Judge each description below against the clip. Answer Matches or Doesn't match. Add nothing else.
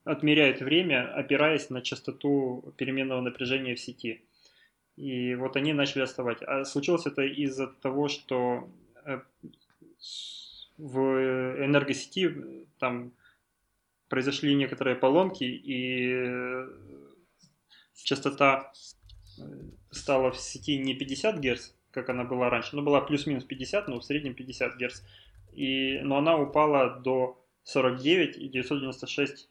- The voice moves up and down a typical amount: Doesn't match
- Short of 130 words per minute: Matches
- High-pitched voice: Doesn't match